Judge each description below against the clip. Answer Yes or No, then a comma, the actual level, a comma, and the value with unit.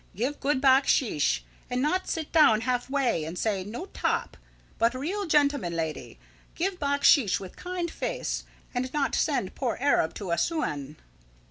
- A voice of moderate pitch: No, very high, 260 Hz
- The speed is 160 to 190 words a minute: No, average, 145 wpm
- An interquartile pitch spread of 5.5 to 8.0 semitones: Yes, wide, 6.7 semitones